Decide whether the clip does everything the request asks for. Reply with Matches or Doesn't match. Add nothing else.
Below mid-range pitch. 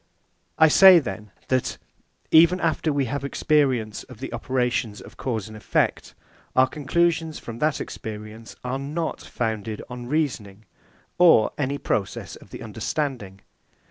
Matches